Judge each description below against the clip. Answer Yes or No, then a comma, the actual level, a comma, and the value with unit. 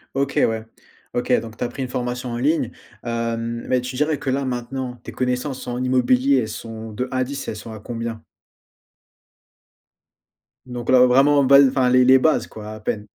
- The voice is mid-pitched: No, low, 125 Hz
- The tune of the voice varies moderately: No, narrow, 2.1 semitones